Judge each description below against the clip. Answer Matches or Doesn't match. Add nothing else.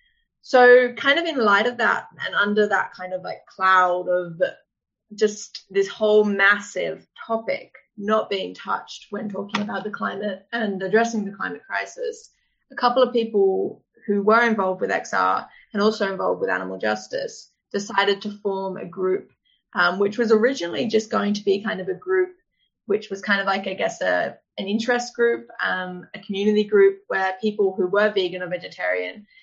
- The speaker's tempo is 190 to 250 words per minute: Doesn't match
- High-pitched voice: Matches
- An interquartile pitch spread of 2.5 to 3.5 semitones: Matches